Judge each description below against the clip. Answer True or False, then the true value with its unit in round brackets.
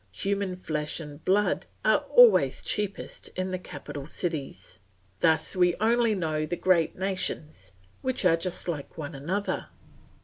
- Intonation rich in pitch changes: False (4.2 semitones)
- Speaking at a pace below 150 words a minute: True (140 wpm)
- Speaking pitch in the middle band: True (175 Hz)